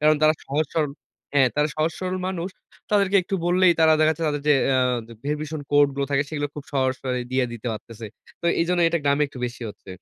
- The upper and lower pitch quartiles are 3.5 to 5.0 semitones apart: Yes, average, 4.0 semitones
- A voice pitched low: No, medium, 150 Hz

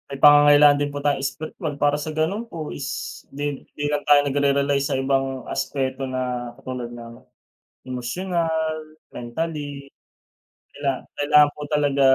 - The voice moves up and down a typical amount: No, narrow, 1.9 semitones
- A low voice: No, medium, 145 Hz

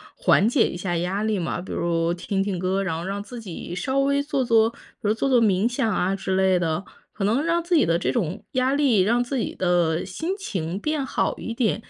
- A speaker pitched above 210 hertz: No, high, 205 Hz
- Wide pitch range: Yes, wide, 5.9 semitones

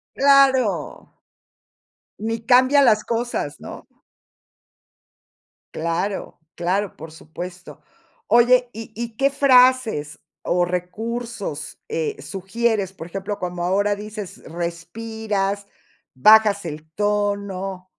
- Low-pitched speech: No, high, 205 Hz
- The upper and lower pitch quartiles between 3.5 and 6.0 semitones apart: Yes, average, 4.6 semitones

